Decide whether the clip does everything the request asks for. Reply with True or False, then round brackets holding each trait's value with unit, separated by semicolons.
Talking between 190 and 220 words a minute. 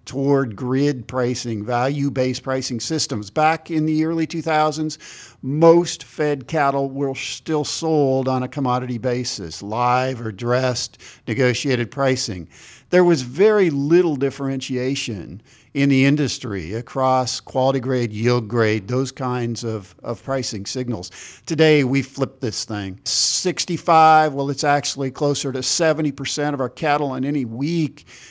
False (135 wpm)